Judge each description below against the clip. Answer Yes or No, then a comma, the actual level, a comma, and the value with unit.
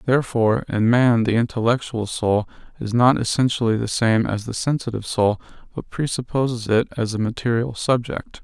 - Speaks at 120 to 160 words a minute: Yes, average, 155 wpm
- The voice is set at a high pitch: No, low, 115 Hz